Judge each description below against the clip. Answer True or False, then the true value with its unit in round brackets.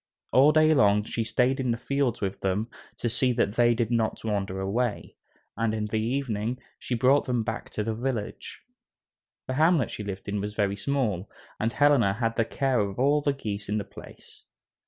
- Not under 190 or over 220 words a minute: True (200 wpm)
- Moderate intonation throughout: True (3.9 semitones)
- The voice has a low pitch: True (115 Hz)